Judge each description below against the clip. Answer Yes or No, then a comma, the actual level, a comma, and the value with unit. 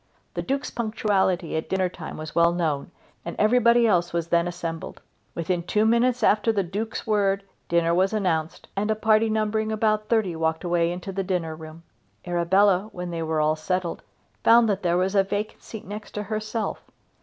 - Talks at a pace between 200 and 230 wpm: No, average, 180 wpm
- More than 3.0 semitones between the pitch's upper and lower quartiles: Yes, average, 4.1 semitones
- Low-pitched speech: No, high, 190 Hz